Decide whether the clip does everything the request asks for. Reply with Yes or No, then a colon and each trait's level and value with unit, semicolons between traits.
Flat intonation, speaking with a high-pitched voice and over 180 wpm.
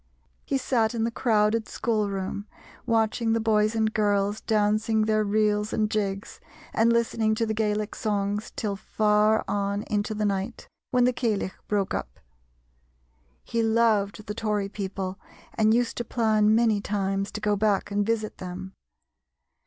No: narrow, 1.6 semitones; high, 215 Hz; average, 155 wpm